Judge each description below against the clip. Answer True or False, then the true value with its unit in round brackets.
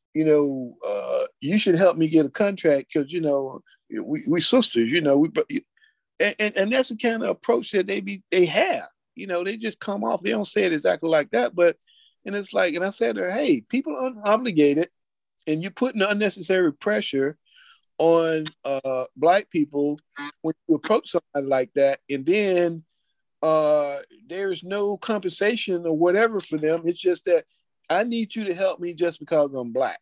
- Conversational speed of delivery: True (190 wpm)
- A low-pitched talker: False (185 Hz)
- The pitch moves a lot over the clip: True (6.3 semitones)